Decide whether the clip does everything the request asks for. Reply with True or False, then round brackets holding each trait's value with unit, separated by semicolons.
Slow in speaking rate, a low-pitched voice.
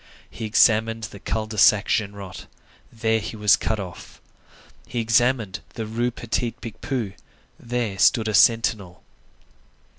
True (130 wpm; 110 Hz)